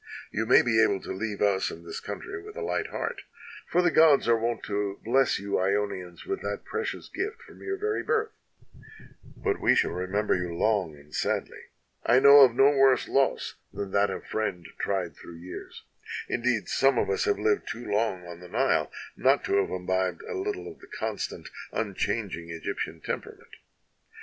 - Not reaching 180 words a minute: No, average, 190 wpm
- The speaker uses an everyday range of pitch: No, wide, 7.2 semitones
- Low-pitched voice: Yes, low, 110 Hz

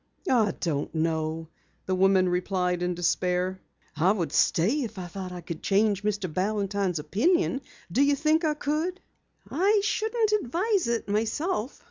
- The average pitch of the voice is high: Yes, high, 200 Hz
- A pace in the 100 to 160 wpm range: Yes, average, 150 wpm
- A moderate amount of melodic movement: No, wide, 8.6 semitones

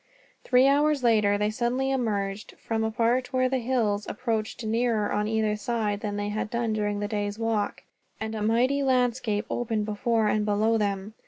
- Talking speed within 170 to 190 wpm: Yes, average, 180 wpm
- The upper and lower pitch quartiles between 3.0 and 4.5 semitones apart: No, narrow, 2.5 semitones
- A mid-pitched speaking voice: No, high, 220 Hz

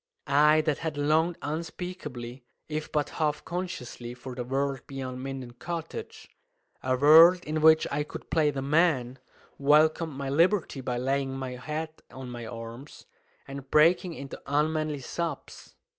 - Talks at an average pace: Yes, average, 145 wpm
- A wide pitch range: No, average, 3.2 semitones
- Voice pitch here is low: No, medium, 145 Hz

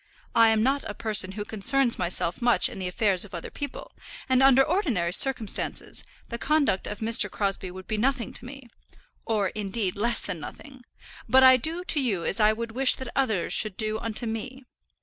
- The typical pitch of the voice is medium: No, high, 225 Hz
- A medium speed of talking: Yes, average, 195 wpm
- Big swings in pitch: No, average, 4.6 semitones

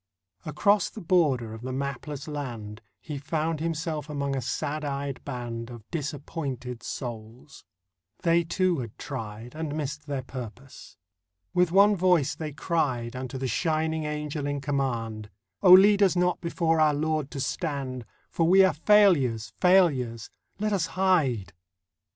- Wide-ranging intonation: No, average, 4.6 semitones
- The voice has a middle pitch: Yes, medium, 145 Hz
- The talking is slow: No, average, 145 wpm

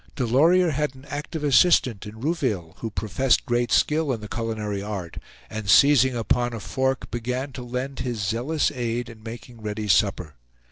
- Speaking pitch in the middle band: No, low, 120 Hz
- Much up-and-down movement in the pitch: No, average, 3.7 semitones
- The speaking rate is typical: Yes, average, 170 wpm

